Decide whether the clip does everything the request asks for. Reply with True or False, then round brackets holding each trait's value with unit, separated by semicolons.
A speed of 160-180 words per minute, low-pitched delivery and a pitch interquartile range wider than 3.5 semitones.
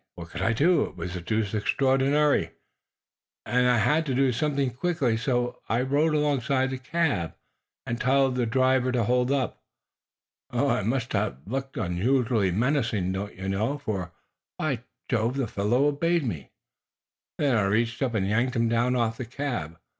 True (165 wpm; 125 Hz; 3.9 semitones)